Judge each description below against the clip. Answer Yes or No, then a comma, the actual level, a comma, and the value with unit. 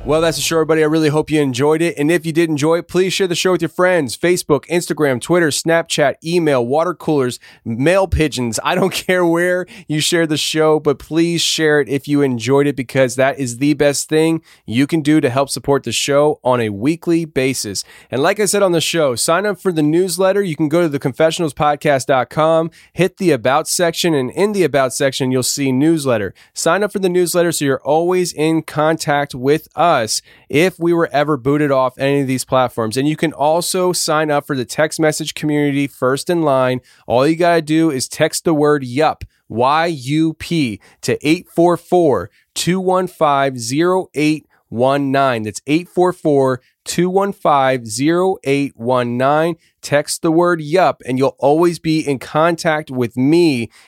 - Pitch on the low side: No, medium, 155 Hz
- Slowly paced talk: No, average, 185 wpm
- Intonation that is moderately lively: Yes, average, 3.6 semitones